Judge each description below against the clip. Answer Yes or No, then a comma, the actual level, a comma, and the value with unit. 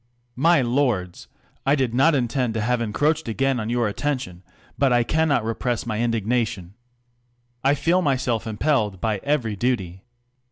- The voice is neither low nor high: No, low, 120 Hz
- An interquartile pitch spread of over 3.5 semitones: Yes, average, 4.0 semitones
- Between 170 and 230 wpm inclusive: No, average, 155 wpm